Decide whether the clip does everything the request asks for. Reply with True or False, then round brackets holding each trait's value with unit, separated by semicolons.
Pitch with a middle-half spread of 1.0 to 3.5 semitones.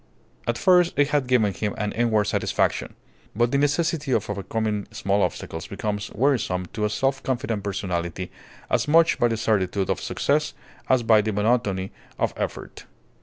False (4.4 semitones)